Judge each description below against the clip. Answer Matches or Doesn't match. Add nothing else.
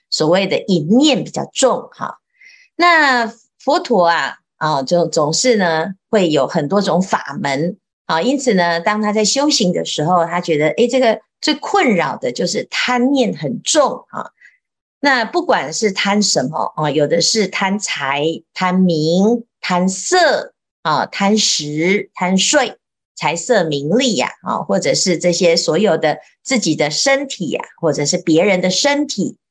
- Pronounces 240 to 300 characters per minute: Doesn't match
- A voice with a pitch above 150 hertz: Matches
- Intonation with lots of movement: Matches